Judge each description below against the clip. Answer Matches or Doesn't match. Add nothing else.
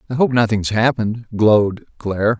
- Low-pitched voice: Matches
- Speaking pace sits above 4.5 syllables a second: Matches